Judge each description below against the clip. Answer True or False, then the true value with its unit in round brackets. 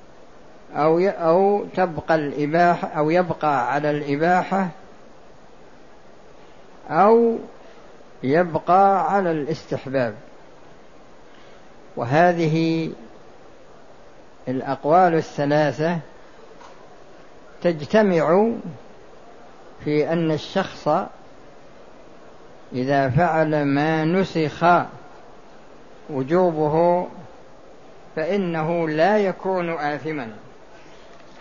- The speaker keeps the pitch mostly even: False (3.2 semitones)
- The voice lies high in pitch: False (165 Hz)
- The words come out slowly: True (50 wpm)